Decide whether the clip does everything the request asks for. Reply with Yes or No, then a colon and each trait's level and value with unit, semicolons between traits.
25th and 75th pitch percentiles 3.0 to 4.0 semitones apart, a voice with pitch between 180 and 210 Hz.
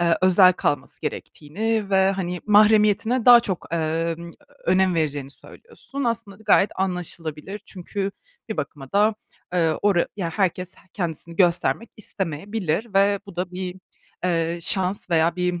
Yes: average, 3.5 semitones; medium, 185 Hz